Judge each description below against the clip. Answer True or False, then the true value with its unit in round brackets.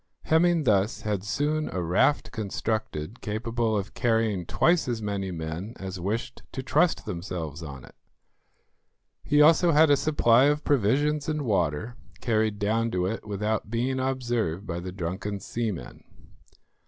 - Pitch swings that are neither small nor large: False (5.7 semitones)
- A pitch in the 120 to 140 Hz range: False (110 Hz)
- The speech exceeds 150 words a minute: False (145 wpm)